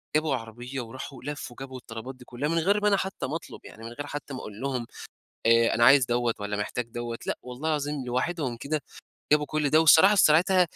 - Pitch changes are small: No, average, 4.3 semitones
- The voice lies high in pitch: No, low, 135 Hz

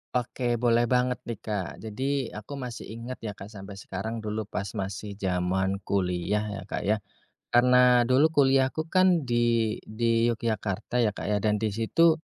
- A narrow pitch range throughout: No, average, 3.6 semitones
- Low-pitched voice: Yes, low, 110 Hz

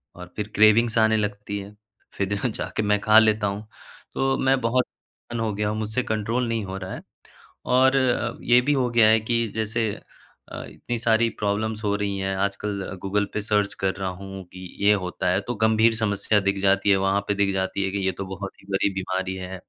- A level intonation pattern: Yes, narrow, 2.3 semitones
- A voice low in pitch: Yes, low, 105 Hz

